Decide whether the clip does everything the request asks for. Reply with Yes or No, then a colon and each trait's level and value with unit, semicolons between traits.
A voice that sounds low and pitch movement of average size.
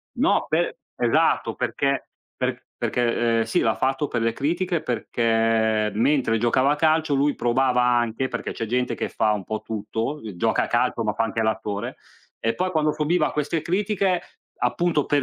Yes: low, 125 Hz; average, 4.9 semitones